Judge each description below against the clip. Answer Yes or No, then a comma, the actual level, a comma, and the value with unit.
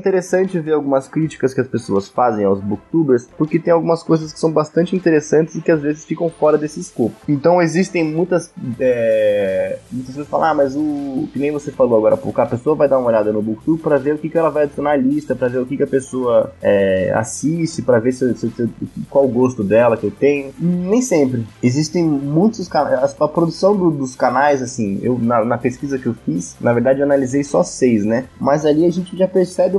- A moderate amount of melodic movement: Yes, average, 4.9 semitones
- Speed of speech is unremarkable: No, fast, 225 wpm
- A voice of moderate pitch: Yes, medium, 150 Hz